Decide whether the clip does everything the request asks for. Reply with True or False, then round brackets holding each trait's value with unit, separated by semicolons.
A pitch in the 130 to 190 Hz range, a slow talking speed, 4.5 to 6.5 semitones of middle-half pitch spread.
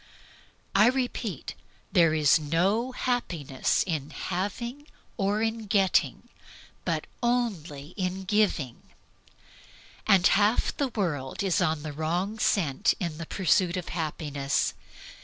True (185 Hz; 105 wpm; 5.4 semitones)